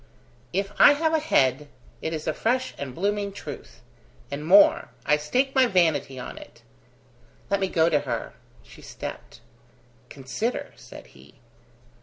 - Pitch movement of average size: No, wide, 7.5 semitones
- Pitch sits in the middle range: Yes, medium, 180 Hz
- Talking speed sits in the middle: Yes, average, 150 wpm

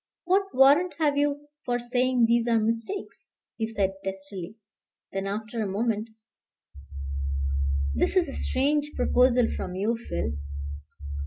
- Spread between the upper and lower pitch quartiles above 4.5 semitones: Yes, wide, 5.4 semitones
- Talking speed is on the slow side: Yes, slow, 130 wpm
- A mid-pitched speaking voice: No, high, 235 Hz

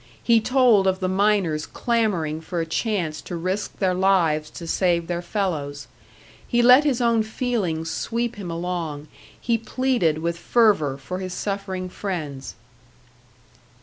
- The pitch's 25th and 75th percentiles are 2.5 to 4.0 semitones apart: No, average, 5.1 semitones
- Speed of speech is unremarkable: Yes, average, 145 wpm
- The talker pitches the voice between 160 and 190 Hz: Yes, medium, 185 Hz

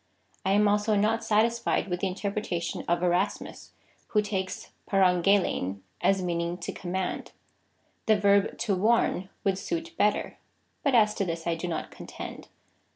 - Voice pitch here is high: Yes, high, 195 Hz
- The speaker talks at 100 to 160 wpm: Yes, average, 155 wpm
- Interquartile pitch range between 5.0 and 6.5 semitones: No, average, 2.9 semitones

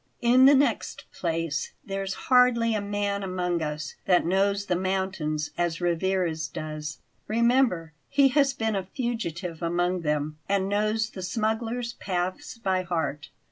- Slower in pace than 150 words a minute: Yes, average, 140 wpm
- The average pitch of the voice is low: No, high, 190 Hz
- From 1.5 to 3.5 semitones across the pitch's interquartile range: No, average, 4.8 semitones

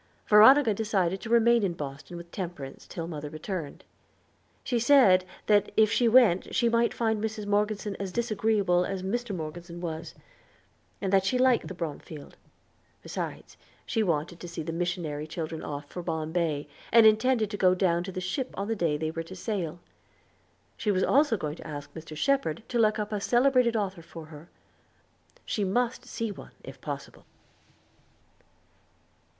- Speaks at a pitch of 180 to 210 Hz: Yes, high, 190 Hz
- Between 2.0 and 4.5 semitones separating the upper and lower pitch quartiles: No, average, 4.9 semitones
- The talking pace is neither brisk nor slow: Yes, average, 165 wpm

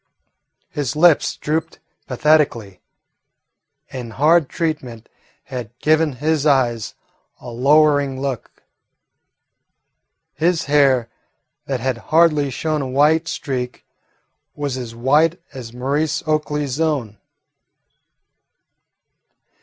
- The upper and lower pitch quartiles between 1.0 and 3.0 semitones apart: No, average, 3.7 semitones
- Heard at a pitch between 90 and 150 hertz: Yes, medium, 140 Hz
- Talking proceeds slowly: Yes, slow, 90 wpm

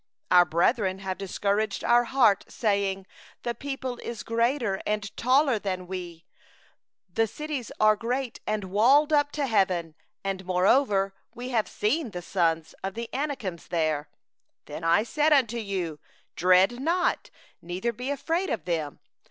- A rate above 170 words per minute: No, average, 150 wpm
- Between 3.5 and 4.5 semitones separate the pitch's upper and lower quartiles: No, average, 5.2 semitones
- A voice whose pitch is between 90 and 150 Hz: No, high, 210 Hz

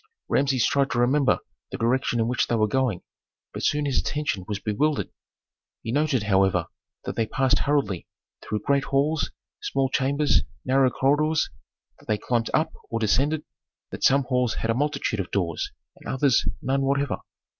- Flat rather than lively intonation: No, average, 3.9 semitones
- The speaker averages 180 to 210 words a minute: No, average, 165 wpm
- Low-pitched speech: Yes, low, 130 Hz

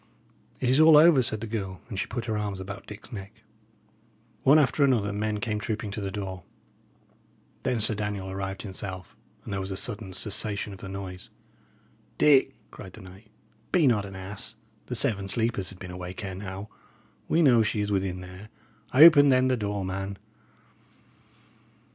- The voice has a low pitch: Yes, low, 105 Hz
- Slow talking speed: No, average, 180 wpm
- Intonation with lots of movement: No, average, 3.3 semitones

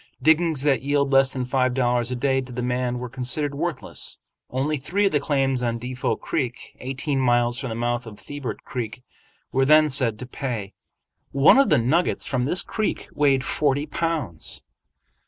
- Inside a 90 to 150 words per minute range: No, average, 180 wpm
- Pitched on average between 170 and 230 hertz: No, low, 130 Hz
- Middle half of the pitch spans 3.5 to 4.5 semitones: No, average, 2.8 semitones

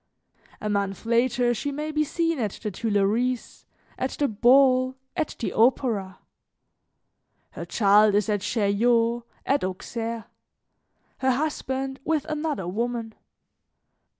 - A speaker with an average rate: No, slow, 120 wpm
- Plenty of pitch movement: No, average, 4.1 semitones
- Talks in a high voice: Yes, high, 240 Hz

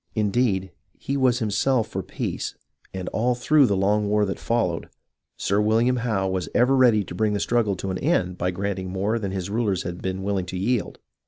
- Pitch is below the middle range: Yes, low, 105 Hz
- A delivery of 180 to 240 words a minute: Yes, average, 200 wpm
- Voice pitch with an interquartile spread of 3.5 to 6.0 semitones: Yes, average, 3.9 semitones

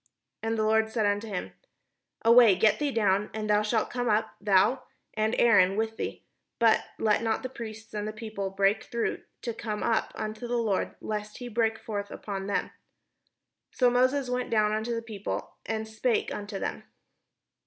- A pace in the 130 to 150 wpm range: No, average, 185 wpm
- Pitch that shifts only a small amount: Yes, narrow, 1.8 semitones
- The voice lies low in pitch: No, high, 220 Hz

